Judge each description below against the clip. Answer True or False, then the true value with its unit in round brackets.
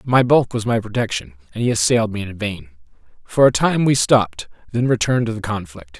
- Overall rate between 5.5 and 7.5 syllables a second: True (5.9 syllables/s)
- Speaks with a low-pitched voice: True (115 Hz)